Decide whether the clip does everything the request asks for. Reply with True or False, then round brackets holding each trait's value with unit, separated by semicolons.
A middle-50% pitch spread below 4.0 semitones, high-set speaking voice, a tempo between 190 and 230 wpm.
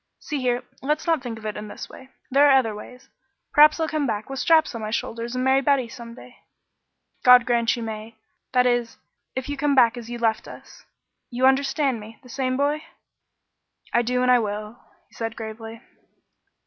True (2.9 semitones; 250 Hz; 200 wpm)